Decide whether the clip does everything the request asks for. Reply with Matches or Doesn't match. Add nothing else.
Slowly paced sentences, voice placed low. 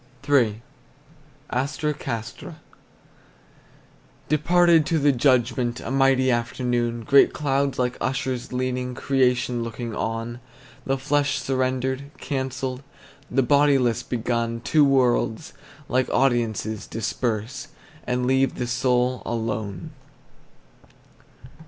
Matches